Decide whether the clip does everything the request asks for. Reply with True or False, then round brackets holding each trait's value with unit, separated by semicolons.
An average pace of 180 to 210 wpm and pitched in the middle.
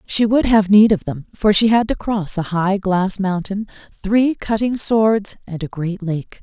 False (205 wpm; 200 Hz)